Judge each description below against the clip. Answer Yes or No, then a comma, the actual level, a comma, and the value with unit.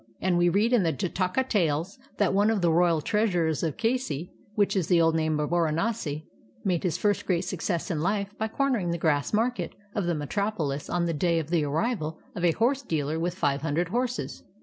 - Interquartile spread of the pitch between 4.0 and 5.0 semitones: Yes, average, 4.5 semitones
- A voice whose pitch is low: No, medium, 175 Hz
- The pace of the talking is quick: Yes, fast, 210 wpm